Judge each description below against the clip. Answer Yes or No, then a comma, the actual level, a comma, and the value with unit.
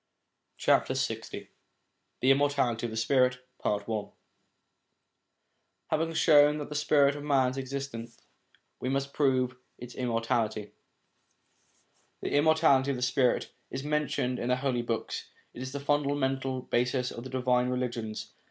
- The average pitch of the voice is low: Yes, low, 130 Hz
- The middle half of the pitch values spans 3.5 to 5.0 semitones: No, narrow, 2.4 semitones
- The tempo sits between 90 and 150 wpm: Yes, slow, 135 wpm